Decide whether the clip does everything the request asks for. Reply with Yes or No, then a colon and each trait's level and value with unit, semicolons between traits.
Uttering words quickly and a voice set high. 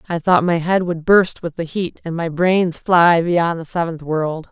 No: fast, 225 wpm; medium, 170 Hz